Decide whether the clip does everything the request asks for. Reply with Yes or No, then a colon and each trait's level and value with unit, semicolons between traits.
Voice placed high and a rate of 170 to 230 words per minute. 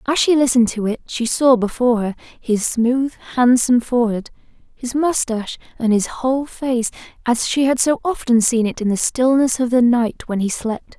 Yes: high, 245 Hz; average, 190 wpm